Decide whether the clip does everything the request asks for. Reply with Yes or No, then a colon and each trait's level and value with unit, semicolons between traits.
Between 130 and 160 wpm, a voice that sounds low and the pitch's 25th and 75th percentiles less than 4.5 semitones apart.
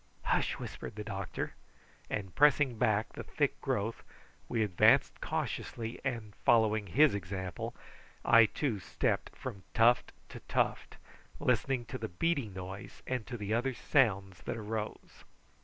Yes: average, 140 wpm; low, 110 Hz; average, 3.5 semitones